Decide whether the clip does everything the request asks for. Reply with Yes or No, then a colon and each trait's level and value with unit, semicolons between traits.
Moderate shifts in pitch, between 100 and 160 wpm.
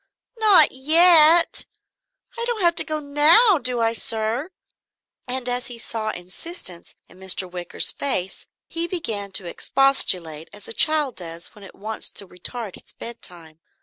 No: wide, 8.6 semitones; average, 150 wpm